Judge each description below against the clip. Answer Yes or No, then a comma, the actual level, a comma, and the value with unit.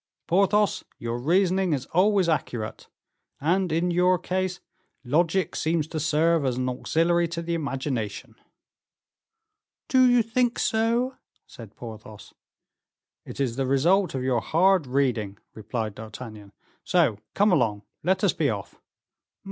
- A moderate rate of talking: No, slow, 130 wpm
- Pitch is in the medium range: Yes, medium, 160 Hz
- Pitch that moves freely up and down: Yes, wide, 7.0 semitones